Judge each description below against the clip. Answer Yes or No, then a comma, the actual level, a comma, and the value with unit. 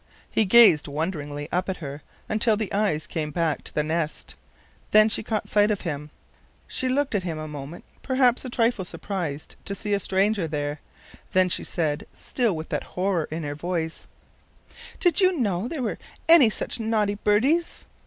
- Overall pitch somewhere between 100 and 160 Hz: No, high, 190 Hz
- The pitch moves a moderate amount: No, wide, 6.0 semitones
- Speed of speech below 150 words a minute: No, average, 180 wpm